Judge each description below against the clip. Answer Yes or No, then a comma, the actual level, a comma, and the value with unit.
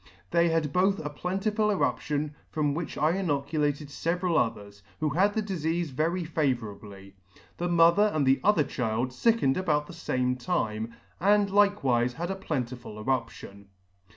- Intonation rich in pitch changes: Yes, wide, 6.0 semitones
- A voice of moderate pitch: Yes, medium, 155 Hz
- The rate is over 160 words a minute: No, average, 155 wpm